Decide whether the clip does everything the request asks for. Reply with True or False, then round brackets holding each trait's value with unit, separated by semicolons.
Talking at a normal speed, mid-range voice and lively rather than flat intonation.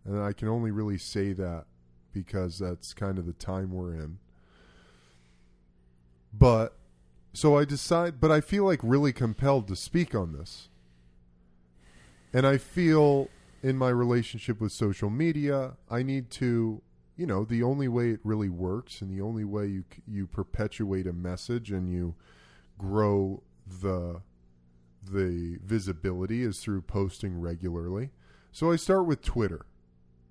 False (145 wpm; 95 Hz; 6.8 semitones)